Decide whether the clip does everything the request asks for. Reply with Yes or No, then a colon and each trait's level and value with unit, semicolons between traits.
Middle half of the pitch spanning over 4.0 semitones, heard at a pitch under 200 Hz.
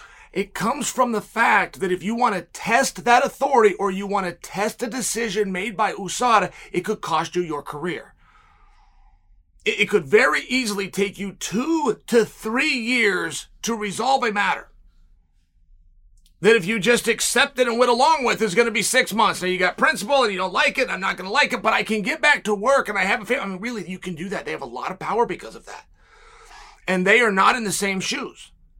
No: average, 4.7 semitones; high, 215 Hz